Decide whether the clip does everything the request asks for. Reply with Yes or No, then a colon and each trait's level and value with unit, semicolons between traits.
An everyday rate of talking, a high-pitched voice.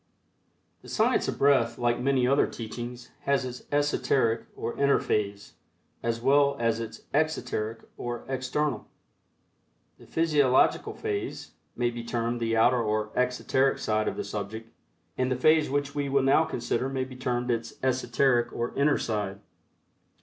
No: average, 150 wpm; low, 125 Hz